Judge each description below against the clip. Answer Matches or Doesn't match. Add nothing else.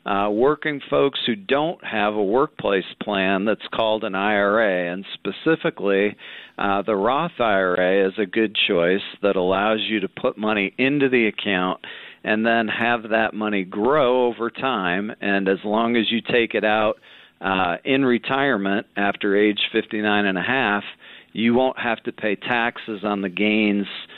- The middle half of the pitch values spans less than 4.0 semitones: Matches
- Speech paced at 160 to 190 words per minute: Matches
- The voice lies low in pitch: Matches